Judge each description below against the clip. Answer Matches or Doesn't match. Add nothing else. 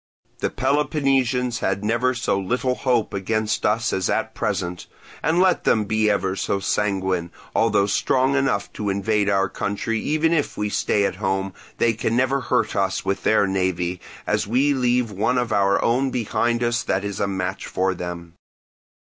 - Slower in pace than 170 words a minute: Doesn't match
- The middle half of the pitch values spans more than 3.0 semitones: Matches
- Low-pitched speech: Matches